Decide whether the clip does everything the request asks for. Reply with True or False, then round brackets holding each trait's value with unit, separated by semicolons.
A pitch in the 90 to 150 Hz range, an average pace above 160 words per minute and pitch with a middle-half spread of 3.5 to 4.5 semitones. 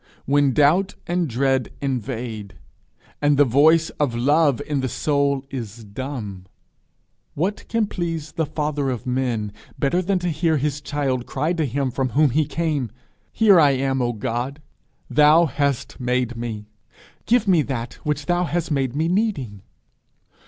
False (140 Hz; 155 wpm; 4.0 semitones)